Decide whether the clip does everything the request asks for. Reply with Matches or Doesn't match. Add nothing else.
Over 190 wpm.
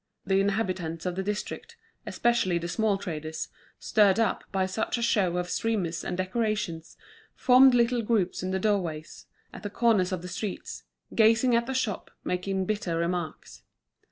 Doesn't match